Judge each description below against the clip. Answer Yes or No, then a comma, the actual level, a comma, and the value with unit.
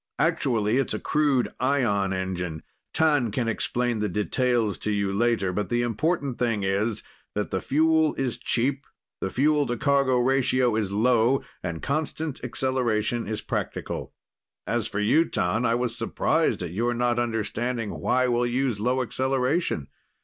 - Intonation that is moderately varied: Yes, average, 3.8 semitones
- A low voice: Yes, low, 120 Hz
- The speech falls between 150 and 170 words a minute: Yes, average, 155 wpm